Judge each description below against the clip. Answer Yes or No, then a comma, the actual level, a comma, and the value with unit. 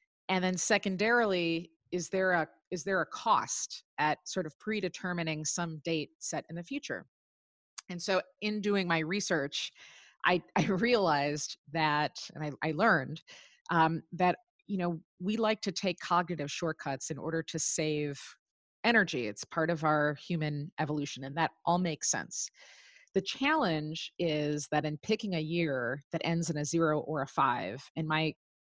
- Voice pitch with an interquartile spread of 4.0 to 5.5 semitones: No, average, 3.5 semitones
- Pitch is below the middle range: No, medium, 165 Hz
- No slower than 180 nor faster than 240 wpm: No, average, 165 wpm